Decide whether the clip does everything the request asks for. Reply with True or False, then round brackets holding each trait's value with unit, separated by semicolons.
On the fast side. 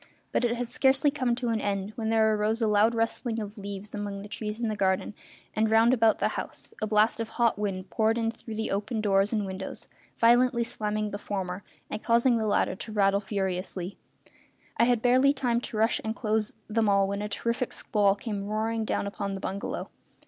True (215 wpm)